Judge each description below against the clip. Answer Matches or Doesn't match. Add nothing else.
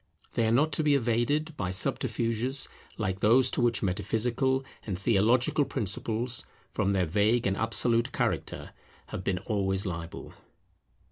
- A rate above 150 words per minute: Doesn't match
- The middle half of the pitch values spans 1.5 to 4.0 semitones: Doesn't match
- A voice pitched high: Doesn't match